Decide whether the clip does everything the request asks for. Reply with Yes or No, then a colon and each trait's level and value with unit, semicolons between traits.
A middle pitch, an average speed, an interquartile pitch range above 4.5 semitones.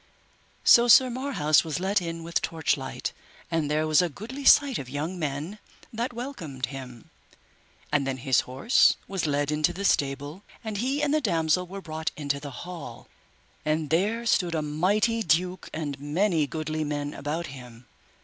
Yes: medium, 160 Hz; average, 170 wpm; average, 5.3 semitones